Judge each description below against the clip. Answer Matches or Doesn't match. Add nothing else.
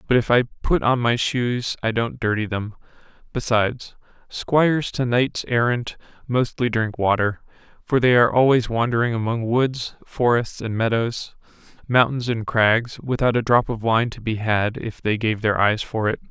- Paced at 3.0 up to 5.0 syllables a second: Matches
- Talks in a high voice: Doesn't match